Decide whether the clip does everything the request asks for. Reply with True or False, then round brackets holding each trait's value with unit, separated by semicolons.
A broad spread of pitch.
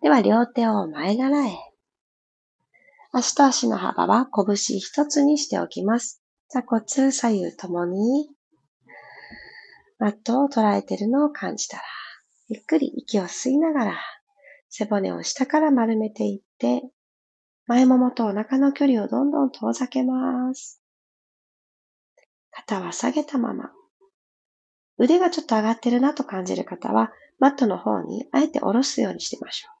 False (4.4 semitones)